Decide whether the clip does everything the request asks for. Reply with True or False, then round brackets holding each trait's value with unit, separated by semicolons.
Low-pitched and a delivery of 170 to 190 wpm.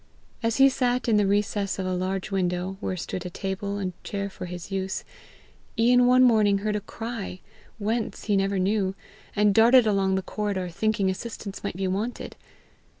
False (200 Hz; 180 wpm)